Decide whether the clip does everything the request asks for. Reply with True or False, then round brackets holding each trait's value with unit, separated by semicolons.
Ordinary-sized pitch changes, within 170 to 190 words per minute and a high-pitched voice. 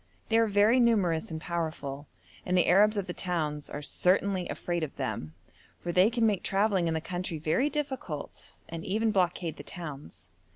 False (4.5 semitones; 180 wpm; 180 Hz)